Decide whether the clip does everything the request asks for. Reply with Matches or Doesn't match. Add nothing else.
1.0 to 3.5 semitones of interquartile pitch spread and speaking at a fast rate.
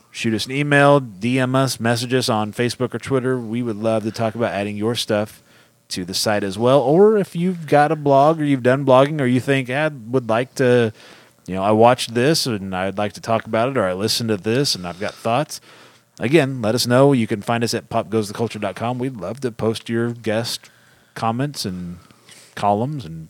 Matches